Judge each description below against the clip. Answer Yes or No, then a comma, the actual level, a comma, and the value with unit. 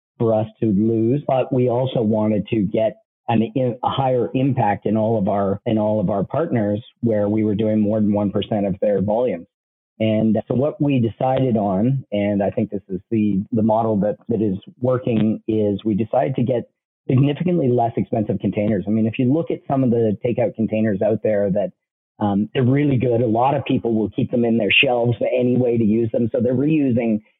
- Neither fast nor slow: No, fast, 210 wpm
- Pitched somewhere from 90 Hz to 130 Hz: Yes, low, 115 Hz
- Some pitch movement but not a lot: Yes, average, 3.1 semitones